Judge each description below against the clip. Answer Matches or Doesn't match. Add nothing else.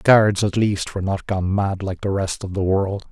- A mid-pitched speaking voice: Doesn't match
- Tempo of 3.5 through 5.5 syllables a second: Matches